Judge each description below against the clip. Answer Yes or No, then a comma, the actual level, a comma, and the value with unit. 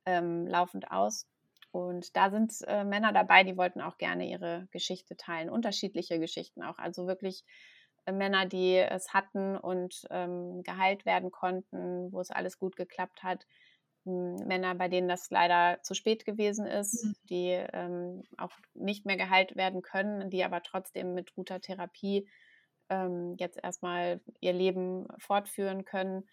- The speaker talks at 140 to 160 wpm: Yes, average, 155 wpm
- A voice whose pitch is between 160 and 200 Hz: Yes, medium, 185 Hz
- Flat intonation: Yes, narrow, 1.4 semitones